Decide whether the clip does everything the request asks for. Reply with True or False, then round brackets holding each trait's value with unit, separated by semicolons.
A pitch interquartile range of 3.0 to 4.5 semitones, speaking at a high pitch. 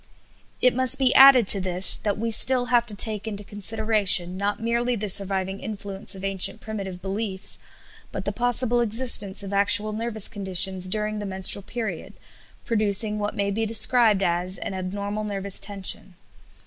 False (2.6 semitones; 205 Hz)